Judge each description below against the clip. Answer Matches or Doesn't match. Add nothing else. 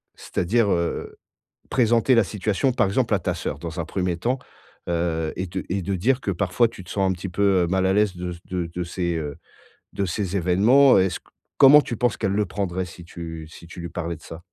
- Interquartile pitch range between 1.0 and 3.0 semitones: Doesn't match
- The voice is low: Matches